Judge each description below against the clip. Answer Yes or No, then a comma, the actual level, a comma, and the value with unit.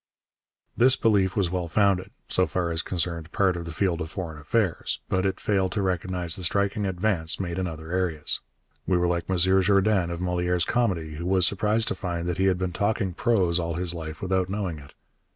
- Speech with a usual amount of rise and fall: No, narrow, 2.2 semitones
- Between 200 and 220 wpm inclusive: Yes, fast, 205 wpm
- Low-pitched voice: Yes, very low, 90 Hz